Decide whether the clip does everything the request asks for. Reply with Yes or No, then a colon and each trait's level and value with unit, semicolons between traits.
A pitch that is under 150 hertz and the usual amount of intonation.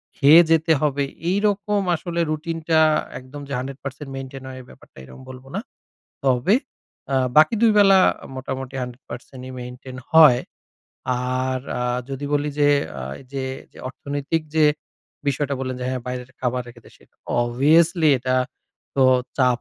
Yes: low, 135 Hz; average, 3.4 semitones